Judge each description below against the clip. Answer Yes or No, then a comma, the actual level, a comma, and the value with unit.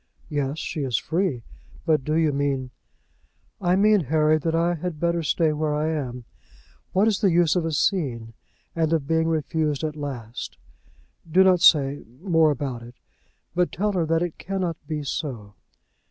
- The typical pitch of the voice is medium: Yes, medium, 155 Hz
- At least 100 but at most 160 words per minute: No, average, 175 wpm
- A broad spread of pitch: No, average, 3.3 semitones